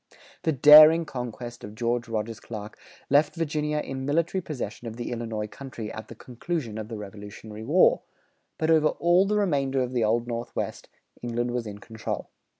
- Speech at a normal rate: Yes, average, 170 wpm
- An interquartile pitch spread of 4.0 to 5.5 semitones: Yes, average, 5.2 semitones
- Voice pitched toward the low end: Yes, low, 120 Hz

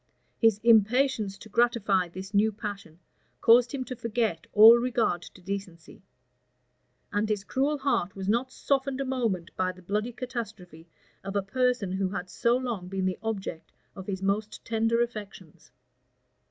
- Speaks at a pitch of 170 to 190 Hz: No, high, 210 Hz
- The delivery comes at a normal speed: Yes, average, 160 wpm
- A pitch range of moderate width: Yes, average, 3.8 semitones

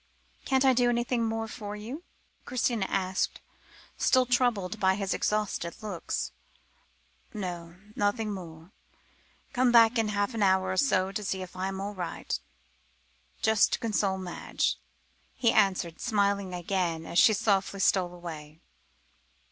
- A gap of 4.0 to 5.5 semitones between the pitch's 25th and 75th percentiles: No, average, 3.3 semitones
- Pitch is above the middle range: Yes, high, 200 Hz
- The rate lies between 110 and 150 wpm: Yes, slow, 135 wpm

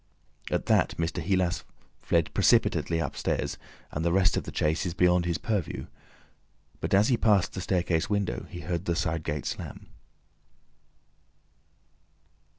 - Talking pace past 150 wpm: No, average, 145 wpm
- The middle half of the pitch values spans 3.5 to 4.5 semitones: No, narrow, 2.5 semitones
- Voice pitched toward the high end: No, very low, 90 Hz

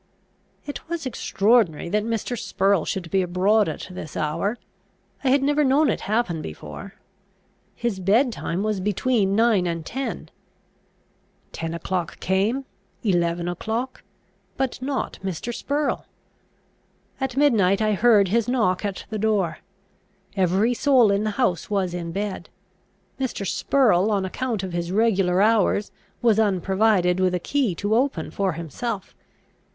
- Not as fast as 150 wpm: Yes, average, 140 wpm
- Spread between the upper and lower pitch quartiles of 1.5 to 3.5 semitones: No, average, 4.6 semitones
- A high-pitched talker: Yes, high, 205 Hz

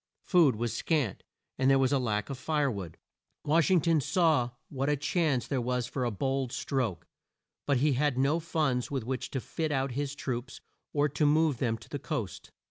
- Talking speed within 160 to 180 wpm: No, fast, 205 wpm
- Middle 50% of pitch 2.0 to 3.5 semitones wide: Yes, average, 3.1 semitones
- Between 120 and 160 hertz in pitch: Yes, low, 135 Hz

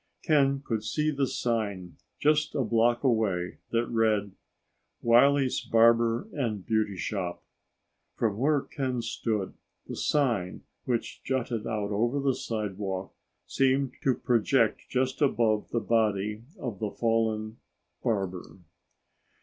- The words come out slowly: Yes, slow, 120 wpm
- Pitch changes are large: No, average, 3.6 semitones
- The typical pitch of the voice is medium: No, low, 115 Hz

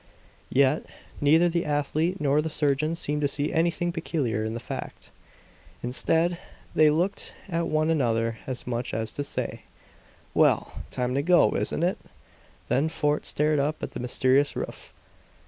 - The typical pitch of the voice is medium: Yes, medium, 150 Hz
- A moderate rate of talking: Yes, average, 155 wpm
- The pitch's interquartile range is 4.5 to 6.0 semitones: No, average, 3.7 semitones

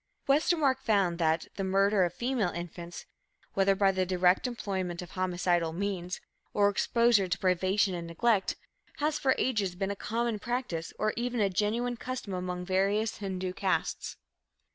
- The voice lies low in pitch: No, high, 195 Hz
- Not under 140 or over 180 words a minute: Yes, average, 155 wpm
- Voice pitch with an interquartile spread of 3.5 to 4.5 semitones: Yes, average, 3.9 semitones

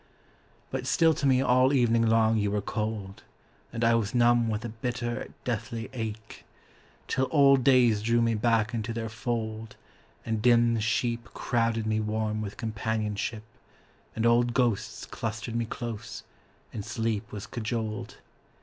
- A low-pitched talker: Yes, low, 115 Hz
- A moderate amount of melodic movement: No, narrow, 1.7 semitones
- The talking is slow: No, average, 150 wpm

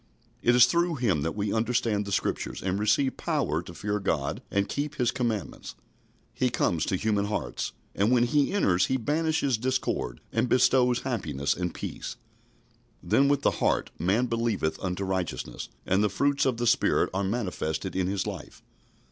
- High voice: No, low, 110 Hz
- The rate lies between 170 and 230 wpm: Yes, average, 175 wpm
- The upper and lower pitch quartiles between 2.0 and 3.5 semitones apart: No, average, 5.2 semitones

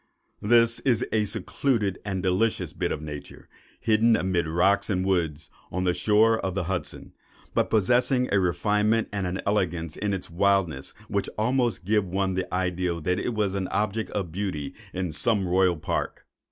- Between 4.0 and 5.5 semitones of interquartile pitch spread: No, average, 3.1 semitones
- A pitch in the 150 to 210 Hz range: No, very low, 95 Hz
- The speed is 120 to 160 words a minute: No, average, 175 wpm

